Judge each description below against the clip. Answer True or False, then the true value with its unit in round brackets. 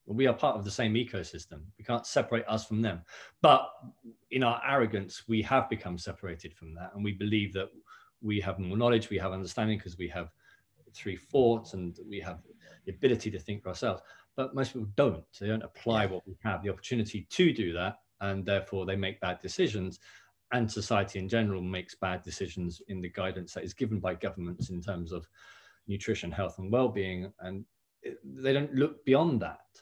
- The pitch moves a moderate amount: True (3.5 semitones)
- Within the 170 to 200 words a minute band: True (195 wpm)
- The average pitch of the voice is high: False (100 Hz)